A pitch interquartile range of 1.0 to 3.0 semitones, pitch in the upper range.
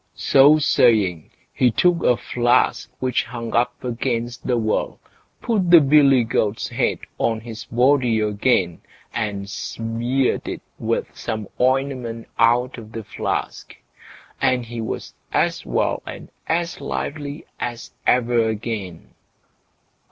No: average, 2.7 semitones; low, 120 Hz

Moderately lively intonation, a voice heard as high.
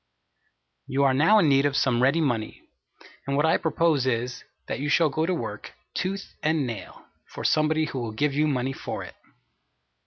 No: average, 3.4 semitones; medium, 140 Hz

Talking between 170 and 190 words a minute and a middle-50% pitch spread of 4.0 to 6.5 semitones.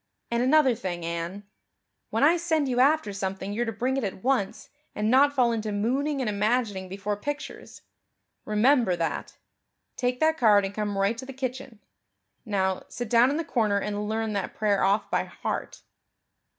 Yes: average, 175 wpm; average, 4.4 semitones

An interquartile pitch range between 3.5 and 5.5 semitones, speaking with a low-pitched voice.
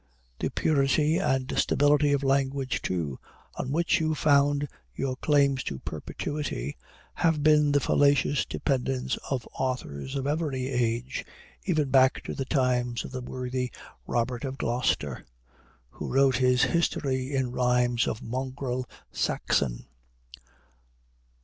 No: narrow, 2.4 semitones; low, 130 Hz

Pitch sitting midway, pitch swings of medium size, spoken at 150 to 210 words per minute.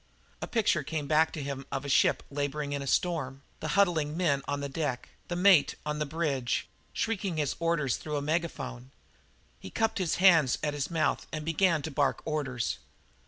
Yes: medium, 150 Hz; average, 3.1 semitones; average, 190 wpm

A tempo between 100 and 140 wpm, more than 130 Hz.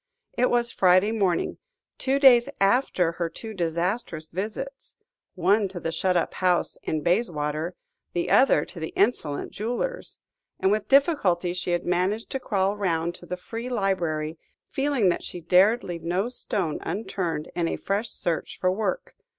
No: average, 160 wpm; medium, 185 Hz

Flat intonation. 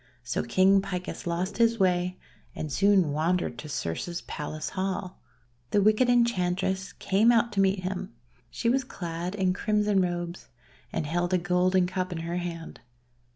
Yes: narrow, 2.2 semitones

